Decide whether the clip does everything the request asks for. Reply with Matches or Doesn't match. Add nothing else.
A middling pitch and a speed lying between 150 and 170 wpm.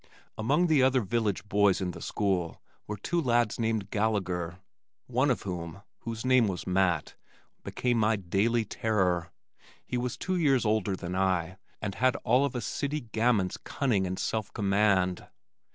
Doesn't match